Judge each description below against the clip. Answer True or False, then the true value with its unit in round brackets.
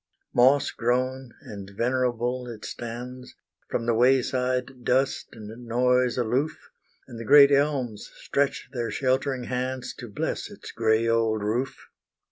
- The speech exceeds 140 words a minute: False (135 wpm)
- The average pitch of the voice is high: False (125 Hz)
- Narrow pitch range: True (2.0 semitones)